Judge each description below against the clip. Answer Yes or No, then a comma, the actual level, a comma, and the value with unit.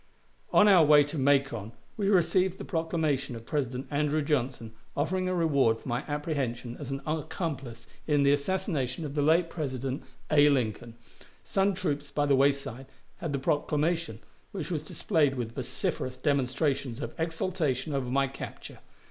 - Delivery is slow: No, average, 155 wpm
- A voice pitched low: No, medium, 145 Hz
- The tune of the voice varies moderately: Yes, average, 3.5 semitones